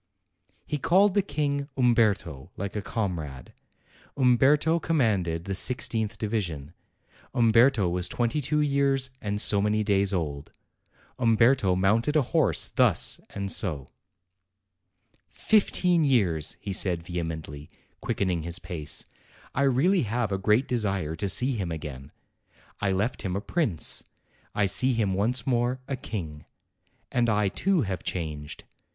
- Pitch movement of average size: No, wide, 6.4 semitones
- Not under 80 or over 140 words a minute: Yes, slow, 135 wpm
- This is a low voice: Yes, low, 105 Hz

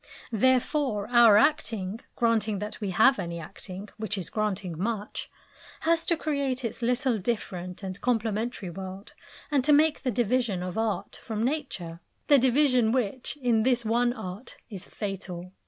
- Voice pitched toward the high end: Yes, high, 225 Hz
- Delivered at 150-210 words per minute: Yes, average, 155 wpm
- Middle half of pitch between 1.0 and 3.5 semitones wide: No, average, 4.6 semitones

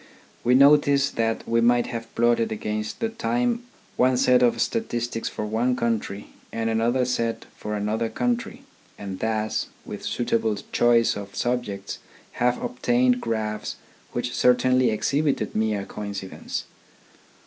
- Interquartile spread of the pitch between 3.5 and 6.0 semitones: No, narrow, 2.5 semitones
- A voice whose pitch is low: Yes, low, 115 Hz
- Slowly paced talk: Yes, slow, 130 wpm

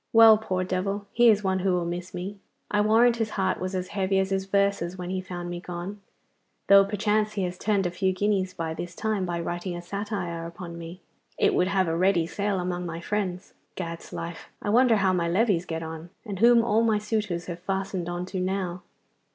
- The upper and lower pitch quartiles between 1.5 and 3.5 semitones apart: Yes, average, 2.7 semitones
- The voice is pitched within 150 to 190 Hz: Yes, medium, 185 Hz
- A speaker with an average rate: No, fast, 215 wpm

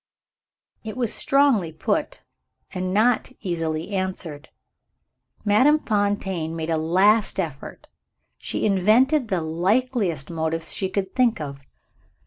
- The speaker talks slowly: Yes, slow, 110 wpm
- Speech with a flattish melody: No, average, 5.1 semitones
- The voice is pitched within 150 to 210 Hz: Yes, high, 190 Hz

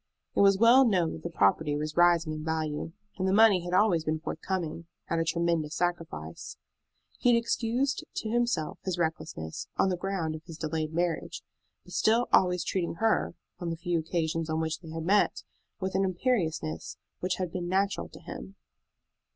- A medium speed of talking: Yes, average, 185 wpm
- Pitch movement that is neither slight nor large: Yes, average, 3.2 semitones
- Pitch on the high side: No, medium, 170 Hz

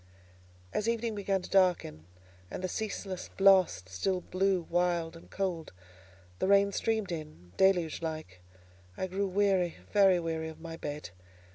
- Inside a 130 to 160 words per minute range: Yes, average, 145 wpm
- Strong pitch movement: No, average, 3.7 semitones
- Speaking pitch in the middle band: Yes, medium, 180 Hz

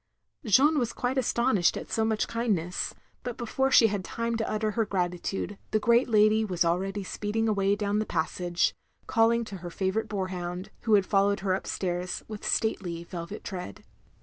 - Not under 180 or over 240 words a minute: Yes, average, 190 wpm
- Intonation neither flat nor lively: Yes, average, 3.4 semitones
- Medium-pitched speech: No, high, 205 Hz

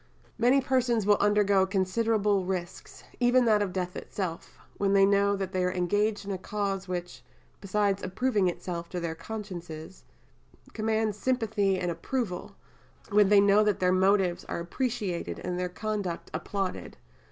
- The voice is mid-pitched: No, high, 200 Hz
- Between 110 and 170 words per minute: Yes, average, 155 wpm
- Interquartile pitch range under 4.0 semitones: Yes, narrow, 2.6 semitones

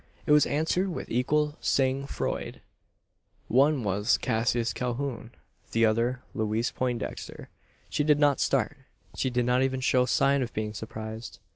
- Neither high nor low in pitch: No, low, 125 Hz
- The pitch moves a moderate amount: Yes, average, 3.6 semitones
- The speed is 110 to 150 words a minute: Yes, average, 145 wpm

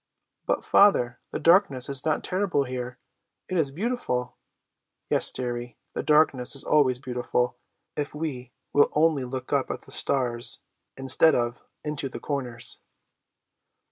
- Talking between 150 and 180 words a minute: No, average, 140 wpm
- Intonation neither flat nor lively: Yes, average, 3.5 semitones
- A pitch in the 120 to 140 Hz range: Yes, low, 135 Hz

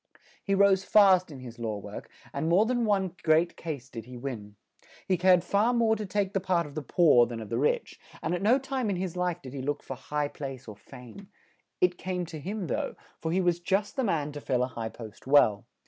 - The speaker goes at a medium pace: No, fast, 240 wpm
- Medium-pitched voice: Yes, medium, 170 Hz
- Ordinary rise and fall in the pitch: No, wide, 6.7 semitones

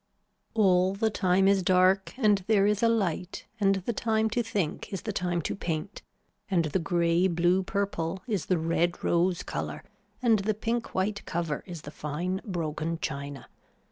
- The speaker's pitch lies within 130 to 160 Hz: No, medium, 185 Hz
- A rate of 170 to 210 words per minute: Yes, average, 175 wpm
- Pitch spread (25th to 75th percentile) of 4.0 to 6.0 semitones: No, average, 3.2 semitones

